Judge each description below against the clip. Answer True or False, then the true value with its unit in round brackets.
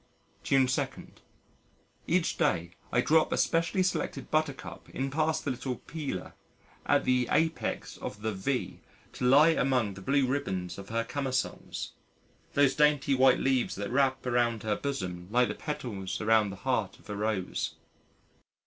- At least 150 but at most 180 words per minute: True (155 wpm)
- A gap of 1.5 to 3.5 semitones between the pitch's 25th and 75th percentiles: False (5.0 semitones)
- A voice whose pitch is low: True (130 Hz)